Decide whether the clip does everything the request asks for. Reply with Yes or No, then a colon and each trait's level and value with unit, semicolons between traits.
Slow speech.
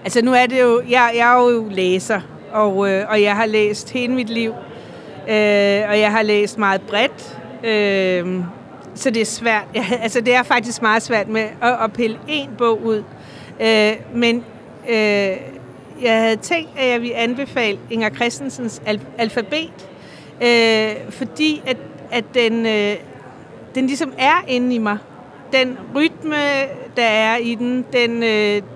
No: average, 165 wpm